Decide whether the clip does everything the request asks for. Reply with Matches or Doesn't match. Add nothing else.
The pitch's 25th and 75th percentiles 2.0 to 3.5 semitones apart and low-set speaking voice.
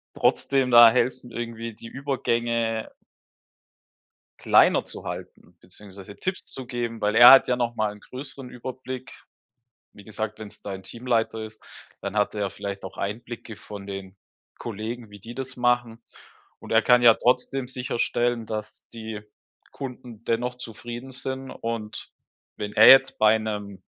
Matches